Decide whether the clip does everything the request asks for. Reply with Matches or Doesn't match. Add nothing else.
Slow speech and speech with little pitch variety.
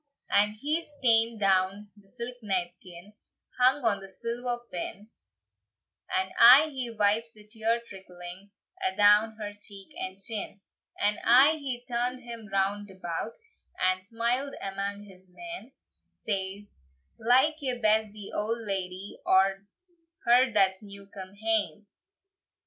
Doesn't match